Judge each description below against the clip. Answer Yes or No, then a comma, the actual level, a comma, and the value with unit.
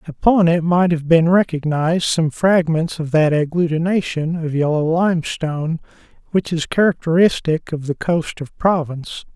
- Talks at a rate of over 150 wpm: No, average, 140 wpm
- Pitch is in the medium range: Yes, medium, 165 Hz